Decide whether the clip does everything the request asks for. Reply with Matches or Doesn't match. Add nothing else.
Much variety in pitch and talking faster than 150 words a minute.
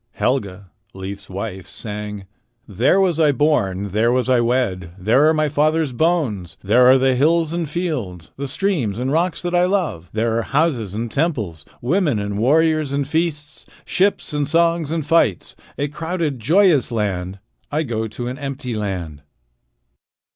Matches